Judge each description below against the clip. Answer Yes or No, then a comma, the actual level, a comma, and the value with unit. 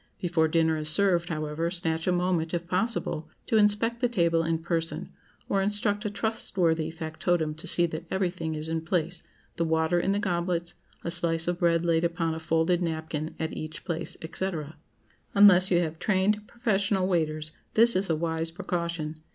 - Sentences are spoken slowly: No, average, 175 wpm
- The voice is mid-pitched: Yes, medium, 170 Hz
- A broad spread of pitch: No, average, 2.7 semitones